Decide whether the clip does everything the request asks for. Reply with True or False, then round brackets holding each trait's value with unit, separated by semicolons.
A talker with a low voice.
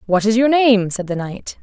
False (215 Hz)